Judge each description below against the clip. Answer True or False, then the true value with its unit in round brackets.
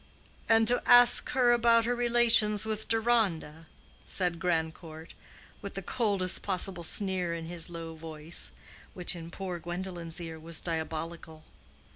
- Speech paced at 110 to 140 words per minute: True (135 wpm)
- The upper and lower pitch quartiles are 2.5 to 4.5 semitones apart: False (5.1 semitones)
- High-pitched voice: False (180 Hz)